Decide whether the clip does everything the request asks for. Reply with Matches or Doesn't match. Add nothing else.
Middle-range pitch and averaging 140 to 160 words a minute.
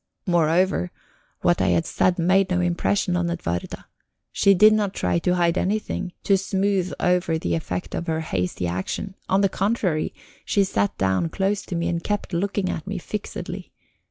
Doesn't match